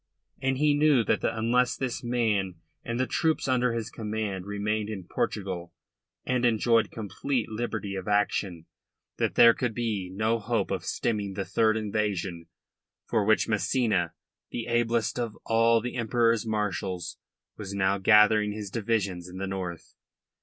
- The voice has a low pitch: Yes, low, 110 Hz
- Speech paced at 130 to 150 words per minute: Yes, average, 145 wpm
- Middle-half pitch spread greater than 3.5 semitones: No, average, 3.0 semitones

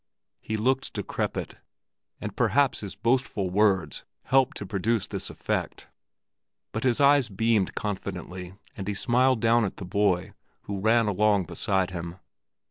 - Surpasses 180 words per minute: No, average, 140 wpm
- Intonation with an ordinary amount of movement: Yes, average, 3.8 semitones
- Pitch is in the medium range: No, low, 105 Hz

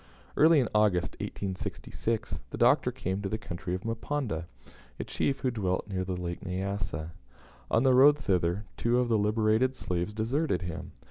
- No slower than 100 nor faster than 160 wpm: No, average, 170 wpm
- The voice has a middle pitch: No, low, 105 Hz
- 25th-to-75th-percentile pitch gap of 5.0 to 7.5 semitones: No, average, 4.5 semitones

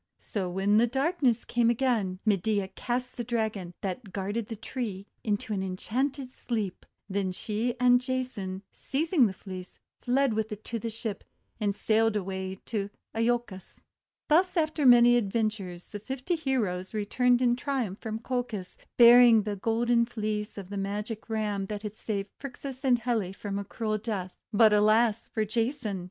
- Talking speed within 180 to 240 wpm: No, average, 160 wpm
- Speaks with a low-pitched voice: No, high, 220 Hz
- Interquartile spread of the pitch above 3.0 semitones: Yes, average, 3.4 semitones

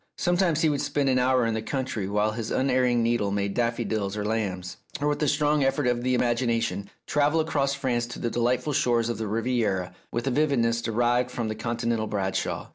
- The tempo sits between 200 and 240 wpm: Yes, fast, 205 wpm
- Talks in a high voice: No, low, 120 Hz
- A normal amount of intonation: Yes, average, 3.3 semitones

